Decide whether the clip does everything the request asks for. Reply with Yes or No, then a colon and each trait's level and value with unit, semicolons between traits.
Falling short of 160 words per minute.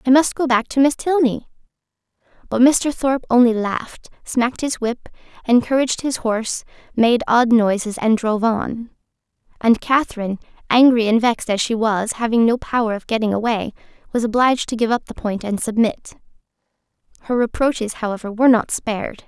No: average, 165 wpm